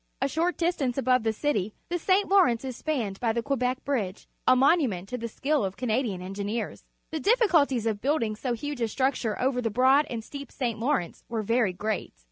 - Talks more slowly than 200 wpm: No, fast, 205 wpm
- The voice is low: No, very high, 250 Hz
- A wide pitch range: No, average, 4.5 semitones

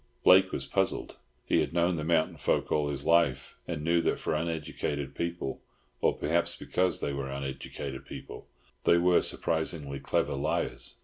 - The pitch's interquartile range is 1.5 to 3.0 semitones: No, average, 3.5 semitones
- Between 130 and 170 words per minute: Yes, average, 150 wpm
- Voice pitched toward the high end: No, very low, 80 Hz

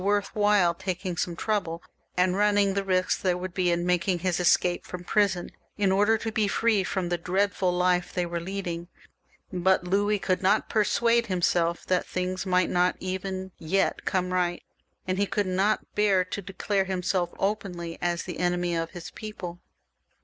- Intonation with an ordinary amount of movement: No, narrow, 2.1 semitones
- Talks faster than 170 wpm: Yes, average, 180 wpm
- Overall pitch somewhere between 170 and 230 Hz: Yes, medium, 185 Hz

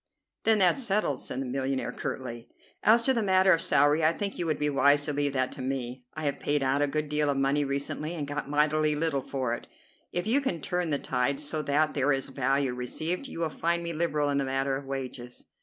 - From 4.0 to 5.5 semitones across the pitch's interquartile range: No, average, 3.3 semitones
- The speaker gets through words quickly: Yes, fast, 240 wpm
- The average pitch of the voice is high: No, medium, 145 Hz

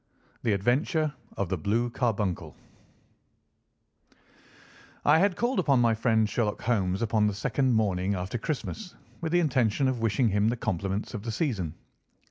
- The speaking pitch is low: Yes, low, 115 Hz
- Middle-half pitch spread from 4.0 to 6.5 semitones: Yes, average, 4.7 semitones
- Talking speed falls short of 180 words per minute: Yes, average, 150 wpm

